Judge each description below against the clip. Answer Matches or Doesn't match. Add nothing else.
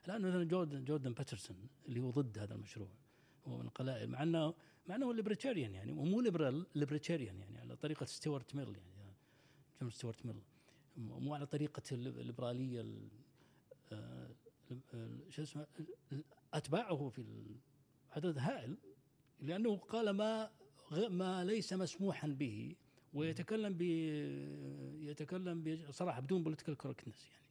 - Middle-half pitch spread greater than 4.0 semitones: Matches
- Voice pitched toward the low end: Doesn't match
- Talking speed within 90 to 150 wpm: Matches